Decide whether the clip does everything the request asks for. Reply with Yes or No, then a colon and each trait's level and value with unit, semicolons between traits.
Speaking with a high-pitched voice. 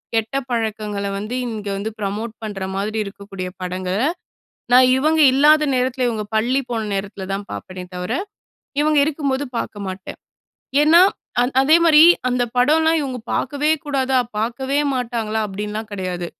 Yes: high, 225 Hz